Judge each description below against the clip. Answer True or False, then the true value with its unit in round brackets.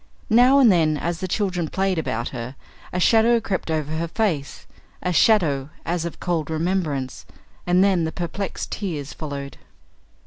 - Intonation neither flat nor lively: True (4.0 semitones)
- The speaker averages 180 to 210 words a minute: False (160 wpm)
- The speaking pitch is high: False (170 Hz)